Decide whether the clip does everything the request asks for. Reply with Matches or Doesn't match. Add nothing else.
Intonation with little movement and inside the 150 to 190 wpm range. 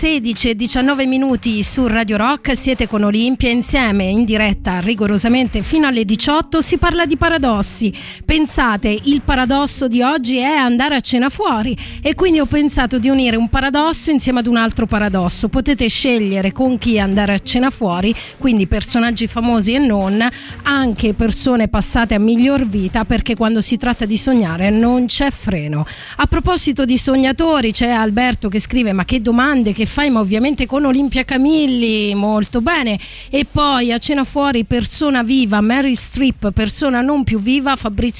Doesn't match